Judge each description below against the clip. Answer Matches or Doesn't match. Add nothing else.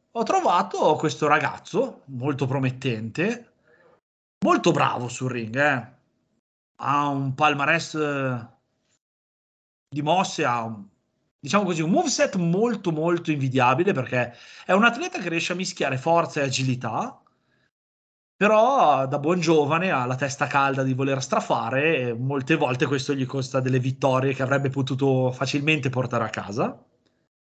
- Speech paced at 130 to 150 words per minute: Matches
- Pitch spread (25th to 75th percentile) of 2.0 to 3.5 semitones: Doesn't match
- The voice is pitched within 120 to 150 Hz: Matches